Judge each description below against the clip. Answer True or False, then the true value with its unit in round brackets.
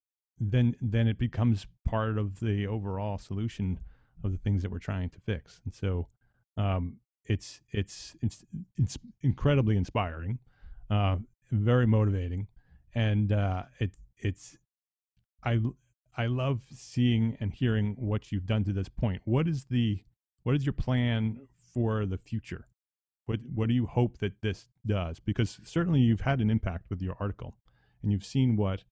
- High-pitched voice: False (110 Hz)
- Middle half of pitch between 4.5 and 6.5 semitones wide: False (3.5 semitones)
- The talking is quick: False (160 wpm)